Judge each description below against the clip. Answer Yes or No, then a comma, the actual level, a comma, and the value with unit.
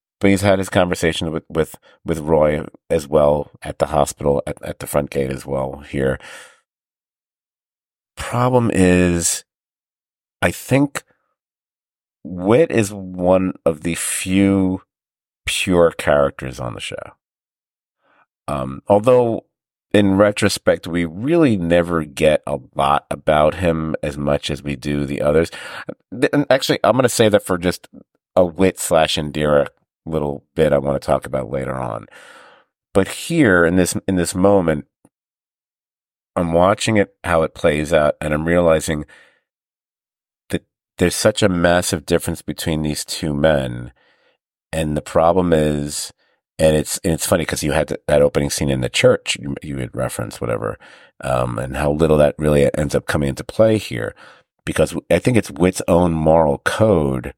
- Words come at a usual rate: Yes, average, 155 wpm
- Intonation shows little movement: No, average, 4.3 semitones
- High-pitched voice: No, very low, 80 Hz